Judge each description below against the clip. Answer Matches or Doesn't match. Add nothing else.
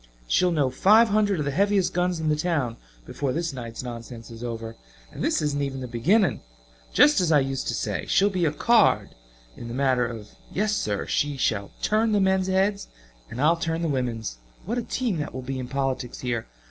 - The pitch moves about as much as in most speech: Doesn't match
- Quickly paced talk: Matches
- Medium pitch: Matches